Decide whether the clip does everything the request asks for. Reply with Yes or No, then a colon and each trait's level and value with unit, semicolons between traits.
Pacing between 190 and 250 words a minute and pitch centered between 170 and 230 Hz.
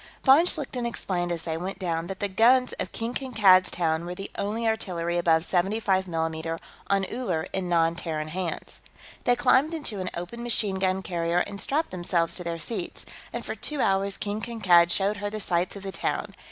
Yes: average, 195 wpm; high, 190 Hz